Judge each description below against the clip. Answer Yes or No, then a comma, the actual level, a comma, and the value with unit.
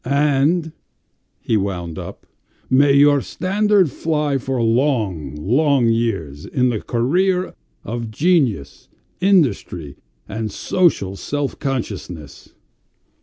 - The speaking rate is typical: No, slow, 100 wpm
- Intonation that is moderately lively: No, wide, 6.8 semitones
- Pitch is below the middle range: Yes, low, 130 Hz